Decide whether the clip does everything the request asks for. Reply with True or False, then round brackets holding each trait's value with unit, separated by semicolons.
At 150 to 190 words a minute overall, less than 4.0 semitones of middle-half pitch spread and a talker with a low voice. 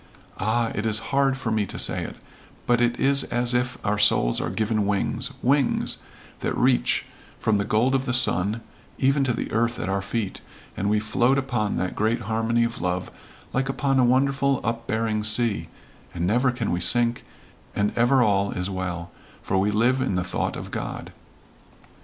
True (185 wpm; 3.5 semitones; 115 Hz)